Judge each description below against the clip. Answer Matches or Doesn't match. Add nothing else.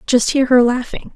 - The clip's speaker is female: Matches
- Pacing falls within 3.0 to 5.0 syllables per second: Matches